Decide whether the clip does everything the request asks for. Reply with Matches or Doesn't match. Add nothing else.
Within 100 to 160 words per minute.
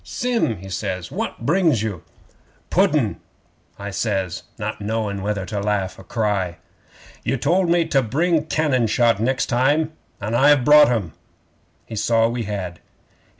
Matches